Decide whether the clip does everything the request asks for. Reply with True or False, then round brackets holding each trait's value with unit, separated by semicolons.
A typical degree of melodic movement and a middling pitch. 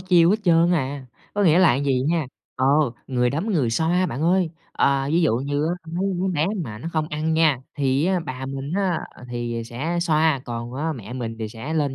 True (4.5 semitones; 150 Hz)